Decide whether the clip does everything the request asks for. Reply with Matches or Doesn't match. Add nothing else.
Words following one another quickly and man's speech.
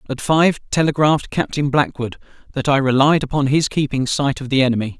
Doesn't match